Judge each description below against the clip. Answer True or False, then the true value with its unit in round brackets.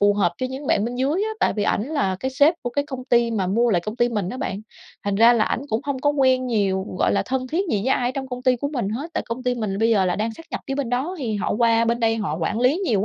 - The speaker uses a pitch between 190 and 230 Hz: False (240 Hz)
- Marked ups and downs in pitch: False (3.7 semitones)